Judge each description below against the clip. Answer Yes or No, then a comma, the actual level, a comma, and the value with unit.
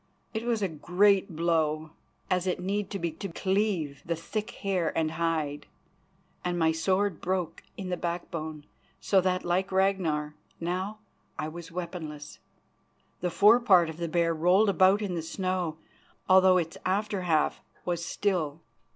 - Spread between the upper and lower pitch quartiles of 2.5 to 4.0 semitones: Yes, average, 2.9 semitones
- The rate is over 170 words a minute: No, average, 150 wpm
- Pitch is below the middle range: No, medium, 180 Hz